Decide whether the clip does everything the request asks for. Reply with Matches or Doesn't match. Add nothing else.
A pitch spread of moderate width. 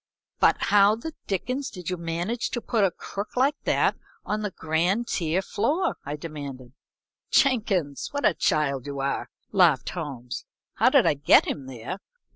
Doesn't match